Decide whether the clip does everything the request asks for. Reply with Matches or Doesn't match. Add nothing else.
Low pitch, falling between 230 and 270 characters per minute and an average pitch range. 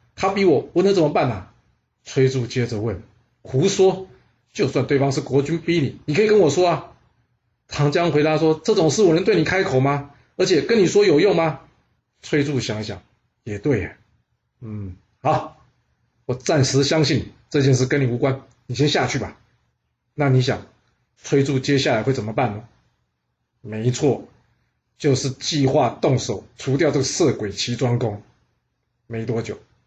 Matches